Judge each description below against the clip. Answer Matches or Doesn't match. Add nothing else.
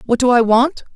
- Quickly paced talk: Matches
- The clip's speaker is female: Matches